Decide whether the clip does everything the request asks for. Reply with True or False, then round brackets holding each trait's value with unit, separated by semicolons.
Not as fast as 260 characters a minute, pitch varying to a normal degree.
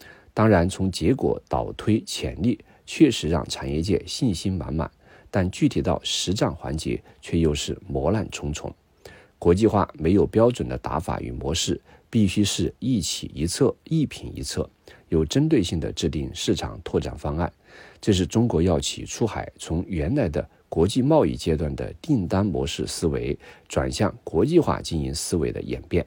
True (250 characters per minute; 4.8 semitones)